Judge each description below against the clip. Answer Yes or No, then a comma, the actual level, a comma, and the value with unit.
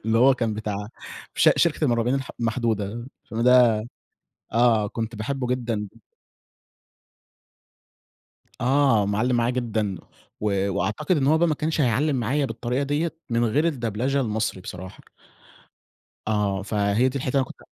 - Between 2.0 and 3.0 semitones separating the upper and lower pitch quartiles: No, average, 3.8 semitones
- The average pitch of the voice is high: No, low, 120 Hz